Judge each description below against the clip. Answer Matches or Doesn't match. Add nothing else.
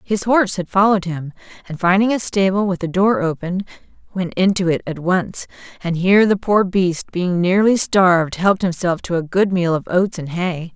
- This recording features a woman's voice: Matches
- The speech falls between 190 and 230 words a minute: Matches